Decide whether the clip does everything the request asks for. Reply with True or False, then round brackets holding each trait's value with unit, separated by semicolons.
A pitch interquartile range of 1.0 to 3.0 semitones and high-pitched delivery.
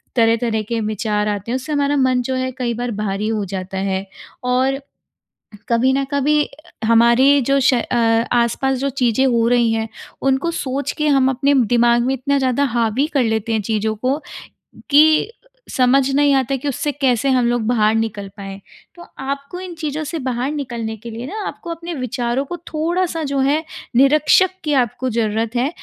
False (3.5 semitones; 255 Hz)